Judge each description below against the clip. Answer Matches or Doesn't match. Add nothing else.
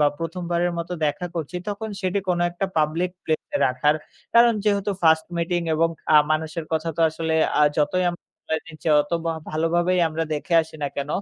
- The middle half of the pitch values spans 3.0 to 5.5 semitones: Doesn't match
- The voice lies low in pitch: Doesn't match